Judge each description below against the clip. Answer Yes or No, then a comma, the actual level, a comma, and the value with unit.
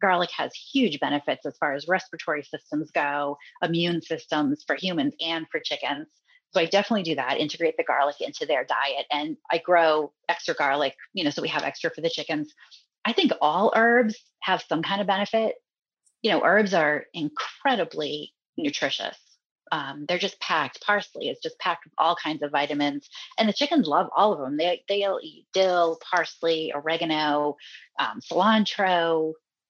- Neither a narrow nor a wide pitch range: No, wide, 5.8 semitones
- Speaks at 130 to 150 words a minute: No, average, 170 wpm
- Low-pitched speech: No, medium, 175 Hz